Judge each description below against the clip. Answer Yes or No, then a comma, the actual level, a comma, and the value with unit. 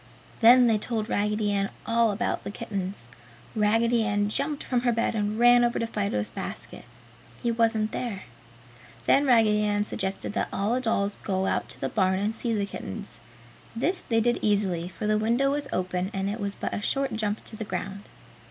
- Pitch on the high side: Yes, high, 215 Hz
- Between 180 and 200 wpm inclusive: Yes, average, 190 wpm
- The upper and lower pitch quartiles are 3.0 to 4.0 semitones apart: No, narrow, 2.6 semitones